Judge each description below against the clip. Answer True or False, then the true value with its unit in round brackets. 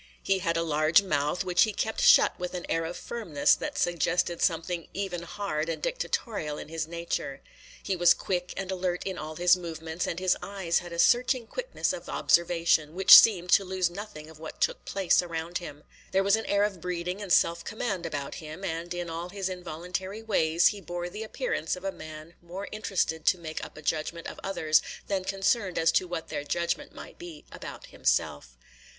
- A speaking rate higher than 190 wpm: True (200 wpm)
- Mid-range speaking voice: True (175 Hz)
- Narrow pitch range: False (3.0 semitones)